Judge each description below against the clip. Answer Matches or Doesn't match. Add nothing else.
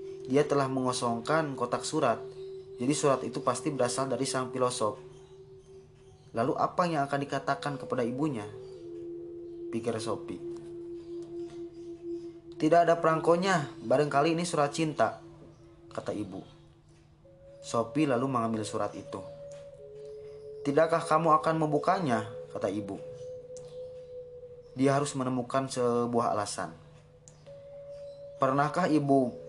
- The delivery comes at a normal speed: Matches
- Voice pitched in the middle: Matches